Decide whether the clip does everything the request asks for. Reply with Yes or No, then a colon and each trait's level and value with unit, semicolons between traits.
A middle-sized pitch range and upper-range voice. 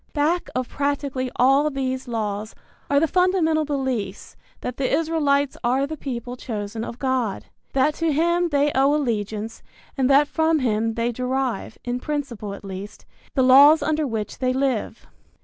Yes: average, 3.9 semitones; very high, 265 Hz